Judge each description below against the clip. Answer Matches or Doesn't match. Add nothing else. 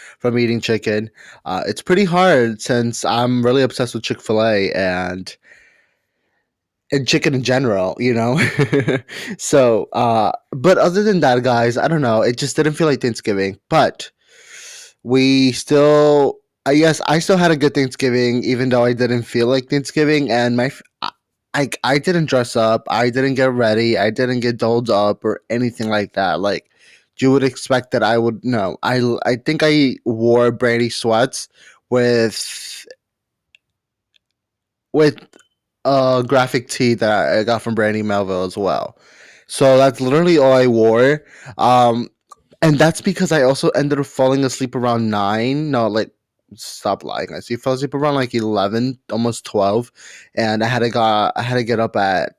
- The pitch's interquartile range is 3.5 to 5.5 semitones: Doesn't match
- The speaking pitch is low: Matches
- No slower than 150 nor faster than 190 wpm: Matches